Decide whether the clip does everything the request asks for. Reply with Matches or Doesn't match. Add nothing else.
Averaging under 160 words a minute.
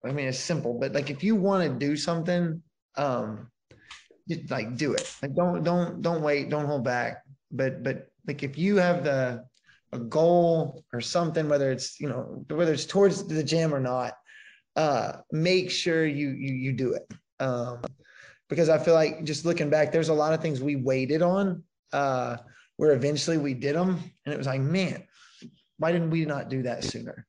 Doesn't match